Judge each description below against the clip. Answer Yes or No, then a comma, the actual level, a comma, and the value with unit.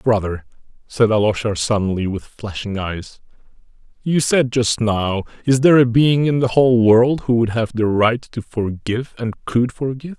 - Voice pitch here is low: Yes, low, 115 Hz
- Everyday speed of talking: Yes, average, 170 wpm